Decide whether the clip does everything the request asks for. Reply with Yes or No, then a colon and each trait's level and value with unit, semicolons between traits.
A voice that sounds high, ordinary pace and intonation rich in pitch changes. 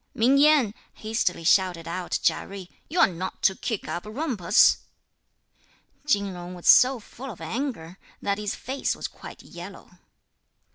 Yes: high, 200 Hz; average, 150 wpm; wide, 5.8 semitones